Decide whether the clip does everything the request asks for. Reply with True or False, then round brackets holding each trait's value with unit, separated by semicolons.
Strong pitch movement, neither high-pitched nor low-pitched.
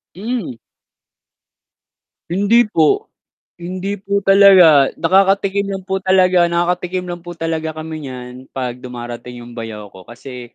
True (7.2 semitones; 170 Hz)